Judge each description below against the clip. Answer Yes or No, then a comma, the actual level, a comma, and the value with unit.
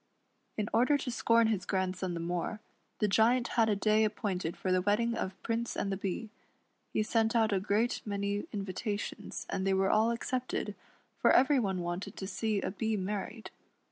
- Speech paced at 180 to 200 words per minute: Yes, average, 185 wpm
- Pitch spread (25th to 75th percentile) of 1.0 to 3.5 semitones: Yes, average, 2.9 semitones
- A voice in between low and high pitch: No, high, 210 Hz